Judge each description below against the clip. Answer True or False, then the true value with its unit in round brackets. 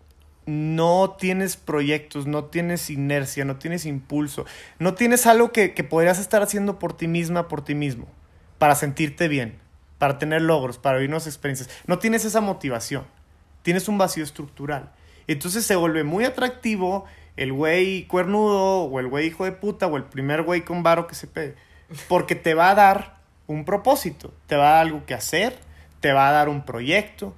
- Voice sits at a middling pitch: True (160 Hz)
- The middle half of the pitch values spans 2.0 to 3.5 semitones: False (4.7 semitones)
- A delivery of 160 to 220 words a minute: True (185 wpm)